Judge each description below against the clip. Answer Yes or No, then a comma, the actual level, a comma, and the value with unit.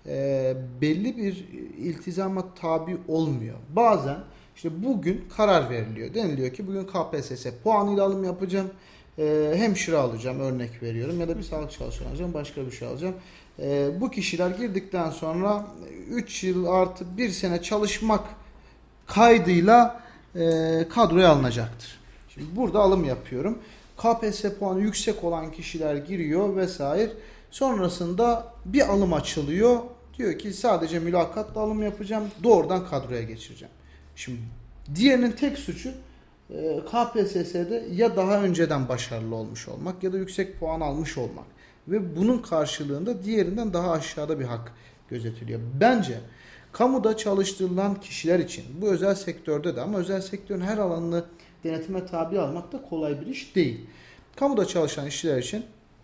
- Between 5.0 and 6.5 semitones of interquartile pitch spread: Yes, wide, 5.6 semitones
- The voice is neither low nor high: Yes, medium, 180 Hz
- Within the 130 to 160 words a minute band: Yes, average, 135 wpm